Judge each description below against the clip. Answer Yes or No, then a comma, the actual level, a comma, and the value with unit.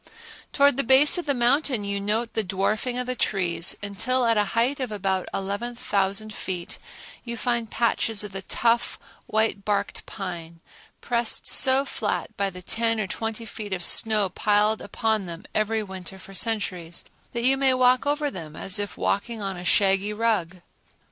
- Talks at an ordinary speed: Yes, average, 175 wpm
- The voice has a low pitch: No, high, 215 Hz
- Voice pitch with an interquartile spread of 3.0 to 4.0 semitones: Yes, average, 3.6 semitones